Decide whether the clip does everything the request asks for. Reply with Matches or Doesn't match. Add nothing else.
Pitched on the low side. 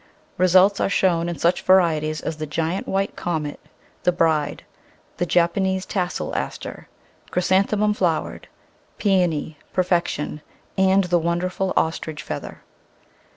Doesn't match